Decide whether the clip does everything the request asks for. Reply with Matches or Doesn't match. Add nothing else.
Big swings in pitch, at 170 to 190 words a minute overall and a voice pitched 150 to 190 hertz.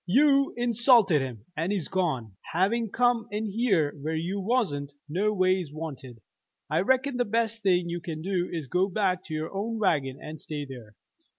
Matches